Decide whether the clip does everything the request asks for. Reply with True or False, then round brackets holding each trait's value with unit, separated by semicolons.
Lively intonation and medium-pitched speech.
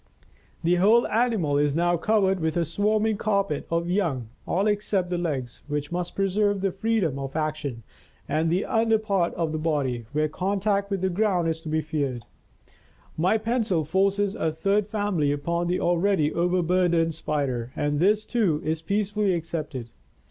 False (4.7 semitones; 175 Hz)